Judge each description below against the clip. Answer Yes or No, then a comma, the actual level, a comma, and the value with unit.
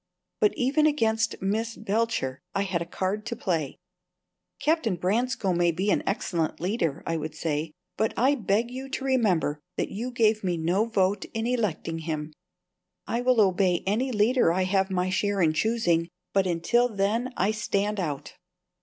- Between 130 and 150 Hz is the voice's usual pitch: No, high, 200 Hz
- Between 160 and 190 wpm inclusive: Yes, average, 170 wpm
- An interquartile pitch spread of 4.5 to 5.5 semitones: Yes, average, 4.9 semitones